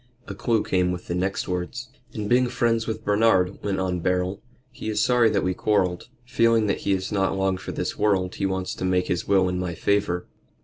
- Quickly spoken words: Yes, fast, 220 wpm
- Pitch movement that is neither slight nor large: Yes, average, 3.0 semitones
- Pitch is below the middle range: Yes, very low, 95 Hz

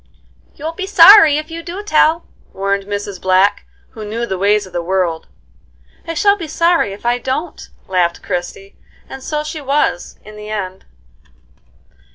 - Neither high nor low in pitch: No, high, 220 Hz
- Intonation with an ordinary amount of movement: No, wide, 8.6 semitones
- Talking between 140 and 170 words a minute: Yes, average, 165 wpm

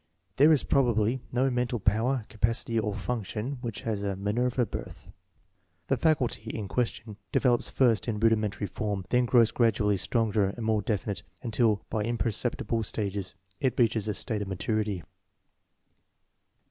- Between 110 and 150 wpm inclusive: Yes, average, 145 wpm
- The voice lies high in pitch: No, low, 110 Hz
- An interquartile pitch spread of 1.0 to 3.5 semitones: Yes, average, 2.8 semitones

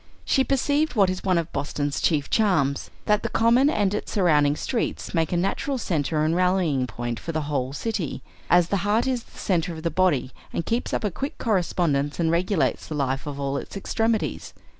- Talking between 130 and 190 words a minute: No, fast, 205 wpm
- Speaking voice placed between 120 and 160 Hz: No, medium, 175 Hz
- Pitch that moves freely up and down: Yes, wide, 6.3 semitones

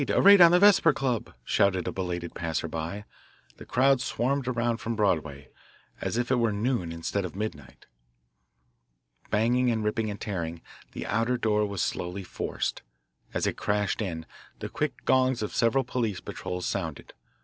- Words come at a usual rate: Yes, average, 165 wpm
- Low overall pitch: Yes, low, 105 Hz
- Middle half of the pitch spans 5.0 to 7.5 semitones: Yes, wide, 5.6 semitones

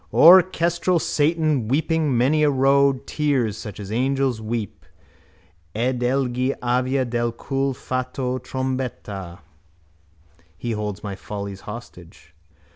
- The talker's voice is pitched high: No, low, 130 Hz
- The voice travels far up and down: No, average, 3.7 semitones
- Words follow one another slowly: Yes, slow, 110 wpm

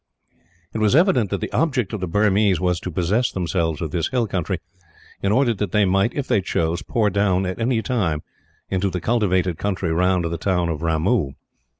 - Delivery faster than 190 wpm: Yes, average, 200 wpm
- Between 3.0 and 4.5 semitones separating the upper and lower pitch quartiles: Yes, average, 3.9 semitones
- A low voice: Yes, very low, 95 Hz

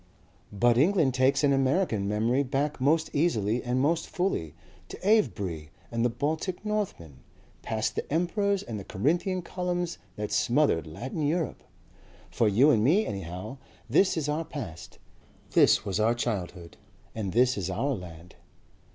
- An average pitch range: No, wide, 7.7 semitones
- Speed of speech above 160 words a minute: No, average, 150 wpm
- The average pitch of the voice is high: No, low, 130 Hz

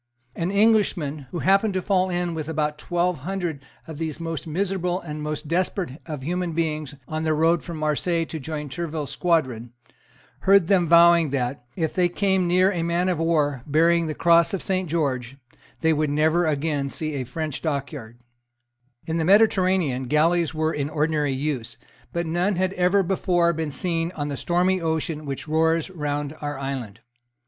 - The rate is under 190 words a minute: Yes, average, 175 wpm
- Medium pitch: Yes, medium, 160 Hz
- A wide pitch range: No, average, 3.0 semitones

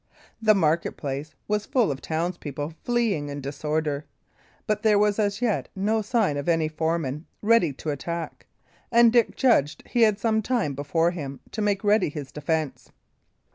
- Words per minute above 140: Yes, average, 165 wpm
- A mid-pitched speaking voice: Yes, medium, 170 Hz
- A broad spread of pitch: Yes, wide, 6.2 semitones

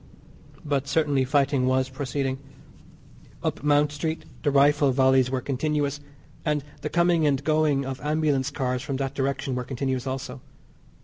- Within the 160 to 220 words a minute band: No, average, 145 wpm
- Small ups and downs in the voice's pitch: Yes, narrow, 2.0 semitones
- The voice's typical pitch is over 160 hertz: No, medium, 140 Hz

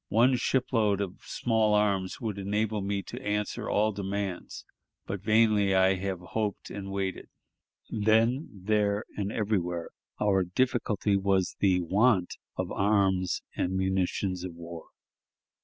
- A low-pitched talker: Yes, low, 100 Hz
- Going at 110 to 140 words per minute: Yes, slow, 135 wpm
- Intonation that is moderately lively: No, narrow, 2.2 semitones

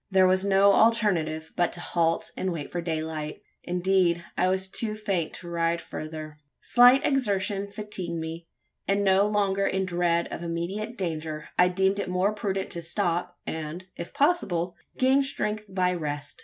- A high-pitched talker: No, medium, 180 Hz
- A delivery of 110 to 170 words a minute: Yes, average, 165 wpm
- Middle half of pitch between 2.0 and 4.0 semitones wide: Yes, average, 3.0 semitones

